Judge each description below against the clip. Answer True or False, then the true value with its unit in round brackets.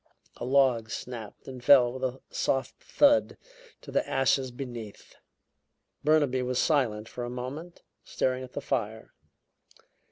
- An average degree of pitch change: False (2.1 semitones)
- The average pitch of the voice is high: False (130 Hz)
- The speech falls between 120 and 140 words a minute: True (135 wpm)